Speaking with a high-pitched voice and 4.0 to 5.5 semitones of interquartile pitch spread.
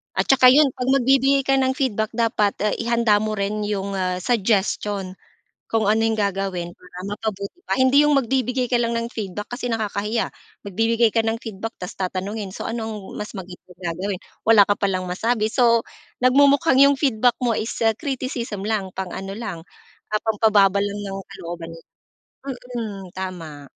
No: high, 215 Hz; average, 3.6 semitones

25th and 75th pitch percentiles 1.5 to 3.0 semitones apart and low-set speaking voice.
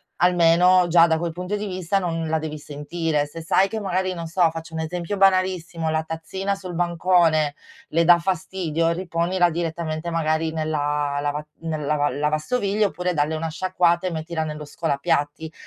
No: narrow, 2.4 semitones; medium, 165 Hz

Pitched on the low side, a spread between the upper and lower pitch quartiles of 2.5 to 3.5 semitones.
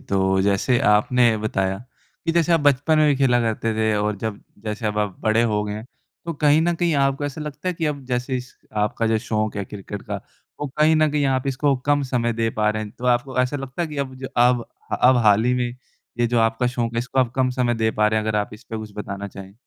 No: low, 120 Hz; average, 4.1 semitones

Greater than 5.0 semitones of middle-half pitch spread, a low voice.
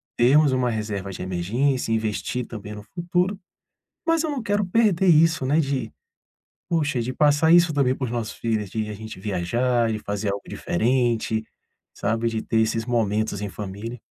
Yes: wide, 5.4 semitones; low, 120 Hz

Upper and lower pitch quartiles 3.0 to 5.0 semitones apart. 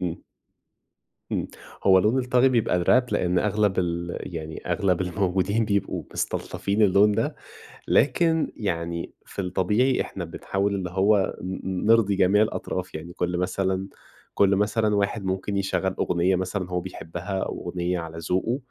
No: narrow, 2.5 semitones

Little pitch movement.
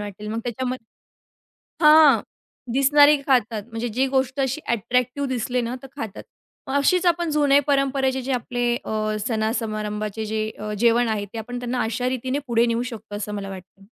No: average, 3.5 semitones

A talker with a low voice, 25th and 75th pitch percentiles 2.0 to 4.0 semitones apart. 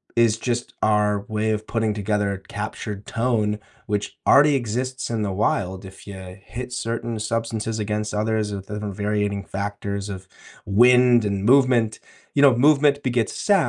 Yes: low, 110 Hz; average, 2.7 semitones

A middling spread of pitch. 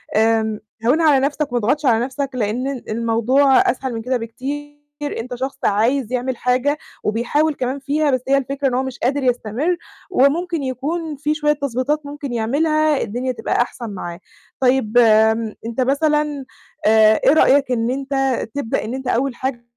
Yes: average, 3.4 semitones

